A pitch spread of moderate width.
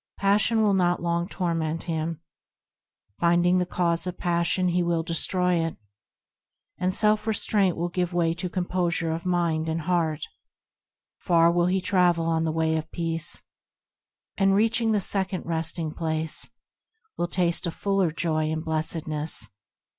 No: narrow, 2.0 semitones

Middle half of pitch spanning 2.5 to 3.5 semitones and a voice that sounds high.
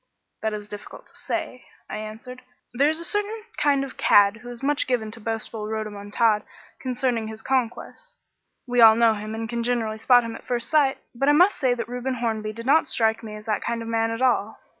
Yes: average, 2.8 semitones; high, 230 Hz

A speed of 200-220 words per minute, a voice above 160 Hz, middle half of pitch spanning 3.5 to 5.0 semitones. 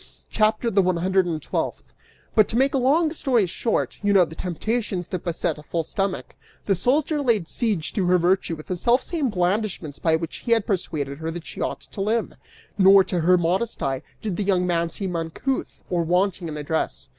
Yes: fast, 205 wpm; medium, 185 Hz; average, 4.6 semitones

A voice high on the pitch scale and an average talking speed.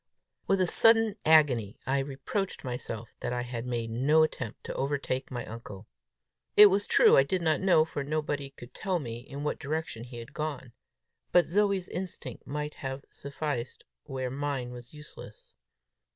No: medium, 140 Hz; average, 165 wpm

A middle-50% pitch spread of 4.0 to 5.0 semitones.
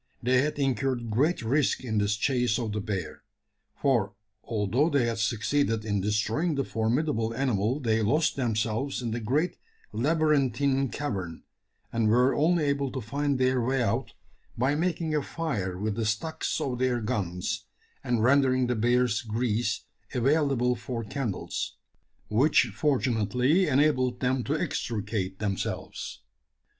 Yes: average, 4.3 semitones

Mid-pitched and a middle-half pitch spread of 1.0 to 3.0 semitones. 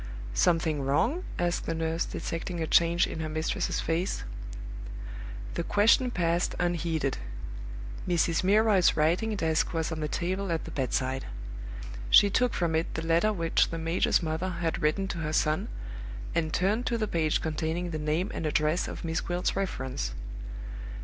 Yes: medium, 165 Hz; narrow, 2.4 semitones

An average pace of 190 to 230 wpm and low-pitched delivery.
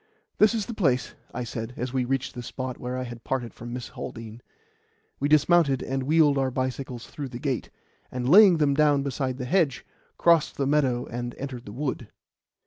Yes: average, 195 wpm; low, 130 Hz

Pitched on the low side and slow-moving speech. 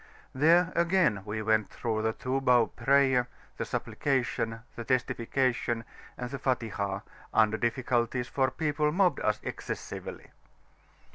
Yes: low, 125 Hz; slow, 125 wpm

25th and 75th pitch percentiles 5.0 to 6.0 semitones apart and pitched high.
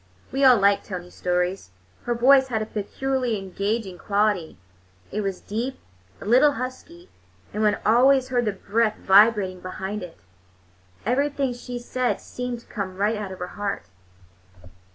No: average, 4.2 semitones; high, 215 Hz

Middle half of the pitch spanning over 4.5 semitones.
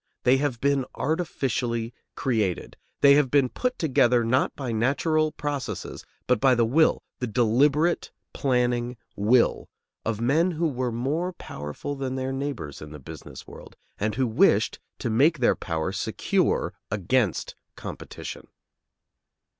No: average, 3.7 semitones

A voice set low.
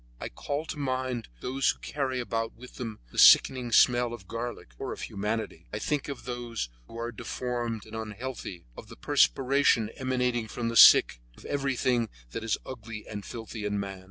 Yes: low, 120 Hz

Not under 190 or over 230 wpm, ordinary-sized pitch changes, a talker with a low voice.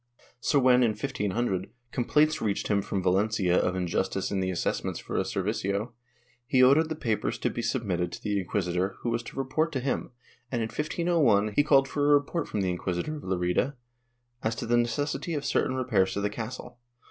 No: average, 195 wpm; wide, 5.9 semitones; low, 115 Hz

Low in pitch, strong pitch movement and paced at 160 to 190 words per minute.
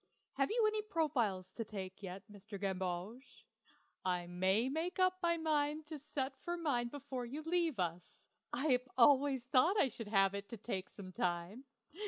No: very high, 250 Hz; wide, 7.8 semitones; average, 165 wpm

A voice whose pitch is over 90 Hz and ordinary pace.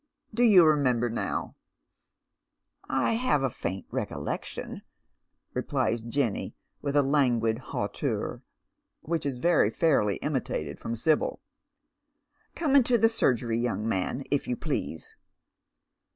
No: low, 135 Hz; slow, 130 wpm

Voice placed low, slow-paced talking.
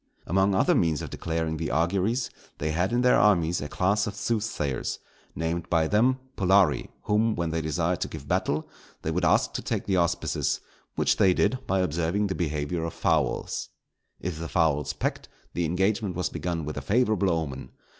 No: very low, 85 Hz; average, 185 wpm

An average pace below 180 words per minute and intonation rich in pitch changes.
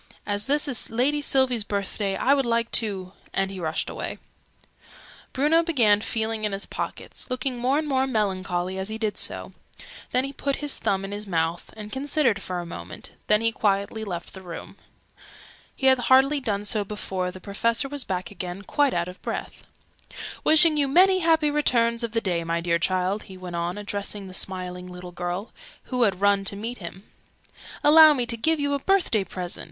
No: average, 195 wpm; wide, 5.9 semitones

